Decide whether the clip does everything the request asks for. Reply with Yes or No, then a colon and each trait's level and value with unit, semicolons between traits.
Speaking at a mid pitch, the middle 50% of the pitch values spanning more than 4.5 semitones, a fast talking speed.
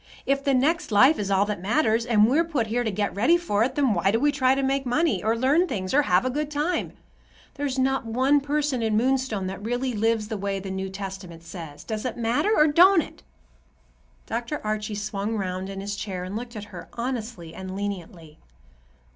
No: high, 225 Hz; average, 5.2 semitones; fast, 215 wpm